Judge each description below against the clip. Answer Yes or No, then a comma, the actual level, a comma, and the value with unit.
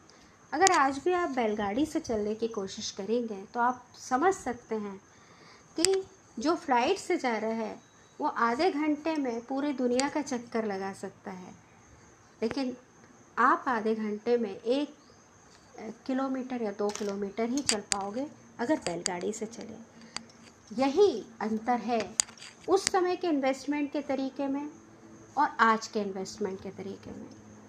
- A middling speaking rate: Yes, average, 145 wpm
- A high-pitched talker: Yes, high, 245 Hz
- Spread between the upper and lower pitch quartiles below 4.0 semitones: No, average, 5.2 semitones